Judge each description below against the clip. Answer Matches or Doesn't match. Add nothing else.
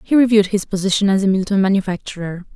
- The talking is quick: Doesn't match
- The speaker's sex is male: Doesn't match